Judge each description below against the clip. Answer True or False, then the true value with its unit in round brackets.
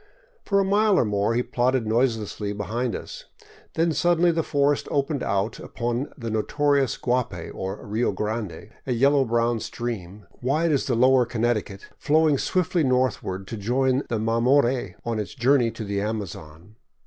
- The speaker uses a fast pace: False (160 wpm)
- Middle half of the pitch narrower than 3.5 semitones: False (4.5 semitones)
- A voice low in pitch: True (120 Hz)